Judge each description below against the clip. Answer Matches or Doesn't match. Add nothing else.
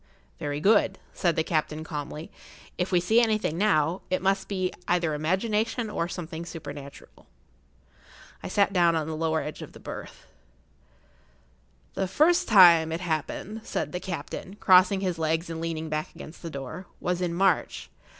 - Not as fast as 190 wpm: Matches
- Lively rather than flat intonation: Doesn't match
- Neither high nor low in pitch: Matches